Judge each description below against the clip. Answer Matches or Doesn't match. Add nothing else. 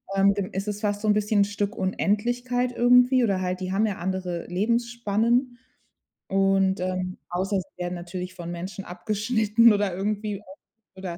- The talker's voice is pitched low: Doesn't match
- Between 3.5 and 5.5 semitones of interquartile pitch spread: Doesn't match